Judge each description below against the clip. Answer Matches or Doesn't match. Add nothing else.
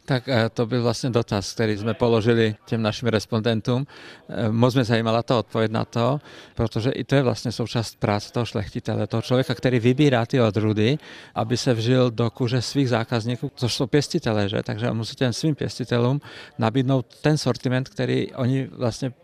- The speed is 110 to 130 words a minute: Doesn't match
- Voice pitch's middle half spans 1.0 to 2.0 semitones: Doesn't match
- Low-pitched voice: Matches